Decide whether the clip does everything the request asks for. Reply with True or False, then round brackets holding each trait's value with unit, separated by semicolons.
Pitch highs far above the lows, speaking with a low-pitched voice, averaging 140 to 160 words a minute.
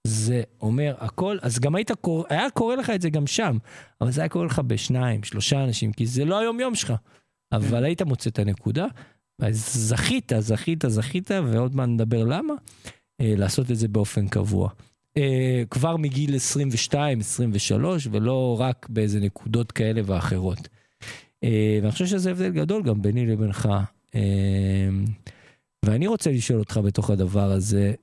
False (5.0 semitones; 120 Hz; 150 wpm)